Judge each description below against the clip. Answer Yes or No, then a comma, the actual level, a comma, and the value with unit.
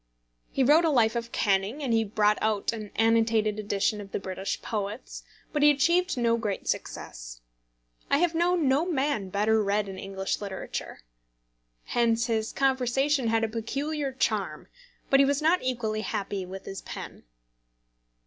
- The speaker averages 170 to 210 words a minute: No, average, 160 wpm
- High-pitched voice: Yes, high, 225 Hz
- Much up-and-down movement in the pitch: No, average, 4.8 semitones